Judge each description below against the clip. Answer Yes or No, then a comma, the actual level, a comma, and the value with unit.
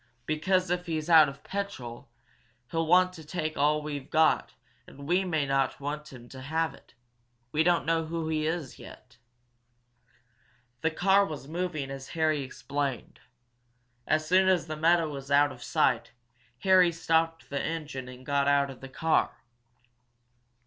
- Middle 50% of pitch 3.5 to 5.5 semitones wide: No, average, 2.8 semitones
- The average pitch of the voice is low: No, medium, 155 Hz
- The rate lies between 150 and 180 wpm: Yes, average, 160 wpm